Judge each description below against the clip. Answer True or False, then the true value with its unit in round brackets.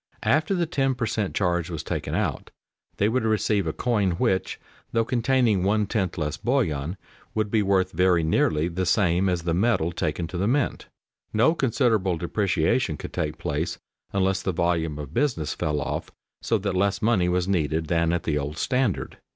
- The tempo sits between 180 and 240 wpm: True (185 wpm)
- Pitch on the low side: True (95 Hz)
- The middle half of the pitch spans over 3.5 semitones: True (5.0 semitones)